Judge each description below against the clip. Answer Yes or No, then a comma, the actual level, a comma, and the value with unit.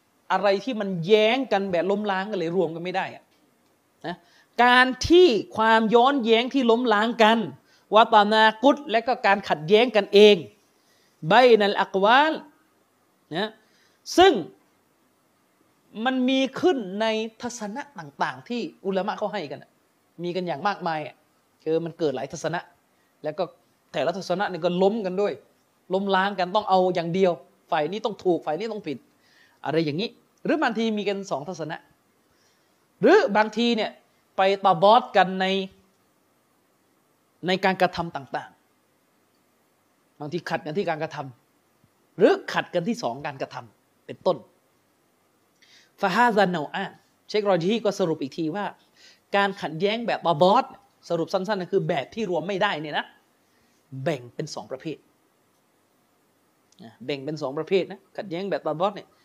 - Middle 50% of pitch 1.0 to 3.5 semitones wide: No, average, 4.3 semitones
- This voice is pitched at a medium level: No, high, 195 Hz